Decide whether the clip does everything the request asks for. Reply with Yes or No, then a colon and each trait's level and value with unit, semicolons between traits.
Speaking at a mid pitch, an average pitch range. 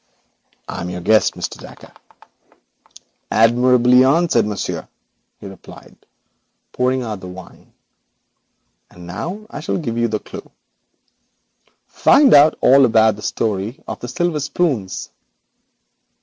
No: low, 120 Hz; average, 4.8 semitones